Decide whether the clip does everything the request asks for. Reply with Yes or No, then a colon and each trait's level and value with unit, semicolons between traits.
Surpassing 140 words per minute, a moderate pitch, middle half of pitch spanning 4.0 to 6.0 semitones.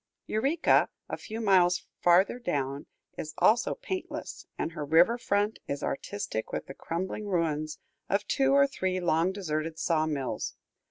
Yes: average, 150 wpm; medium, 180 Hz; wide, 5.4 semitones